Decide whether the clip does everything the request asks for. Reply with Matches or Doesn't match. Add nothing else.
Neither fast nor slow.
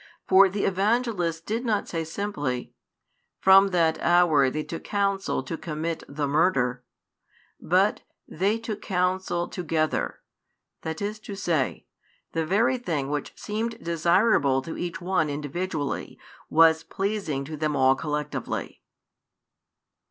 Doesn't match